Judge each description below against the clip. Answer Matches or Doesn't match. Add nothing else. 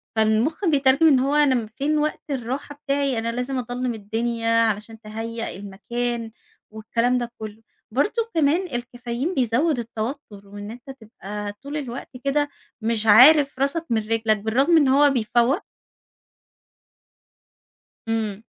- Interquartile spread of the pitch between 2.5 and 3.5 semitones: Doesn't match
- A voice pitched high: Matches